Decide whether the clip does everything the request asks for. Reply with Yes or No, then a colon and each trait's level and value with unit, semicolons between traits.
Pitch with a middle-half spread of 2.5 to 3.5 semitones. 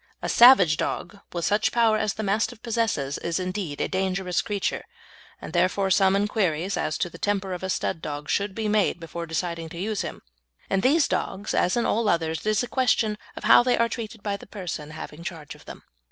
No: average, 4.0 semitones